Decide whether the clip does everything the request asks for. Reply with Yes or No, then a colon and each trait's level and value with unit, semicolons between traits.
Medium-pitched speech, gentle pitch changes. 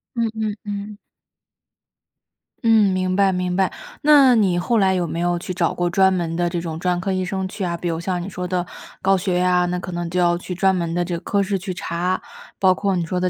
Yes: medium, 180 Hz; narrow, 1.7 semitones